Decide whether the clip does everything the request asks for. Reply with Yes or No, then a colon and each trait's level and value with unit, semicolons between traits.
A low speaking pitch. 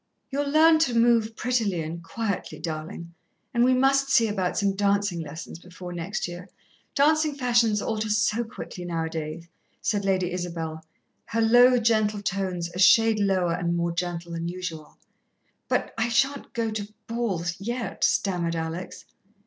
No: high, 200 Hz